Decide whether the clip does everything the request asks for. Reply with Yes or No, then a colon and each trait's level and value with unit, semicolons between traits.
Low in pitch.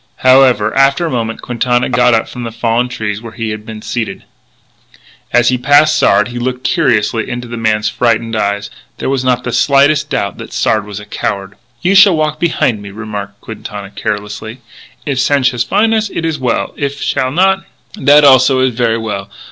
Yes: low, 120 Hz